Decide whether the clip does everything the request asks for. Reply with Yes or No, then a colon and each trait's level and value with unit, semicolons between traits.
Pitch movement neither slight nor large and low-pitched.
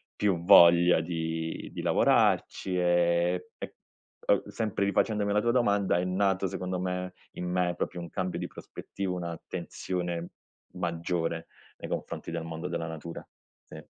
No: narrow, 1.8 semitones; very low, 90 Hz